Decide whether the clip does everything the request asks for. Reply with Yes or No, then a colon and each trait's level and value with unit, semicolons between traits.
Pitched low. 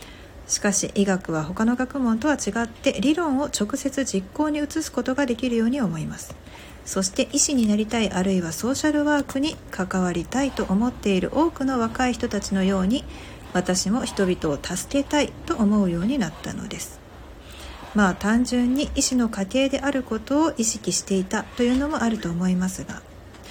No: high, 220 Hz